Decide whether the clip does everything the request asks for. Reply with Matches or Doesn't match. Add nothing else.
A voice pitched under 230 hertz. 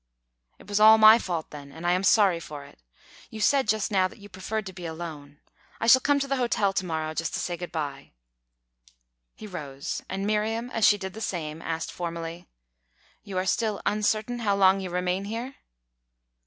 Matches